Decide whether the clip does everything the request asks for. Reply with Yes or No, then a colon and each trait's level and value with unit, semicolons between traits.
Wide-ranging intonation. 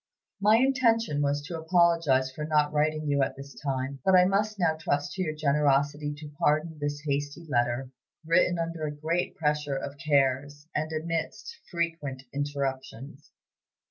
No: average, 2.9 semitones